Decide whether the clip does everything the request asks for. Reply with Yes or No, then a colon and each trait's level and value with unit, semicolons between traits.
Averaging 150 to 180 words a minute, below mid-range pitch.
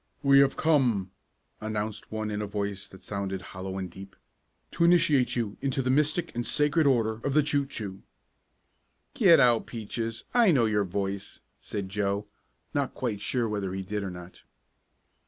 Yes: average, 170 wpm; low, 110 Hz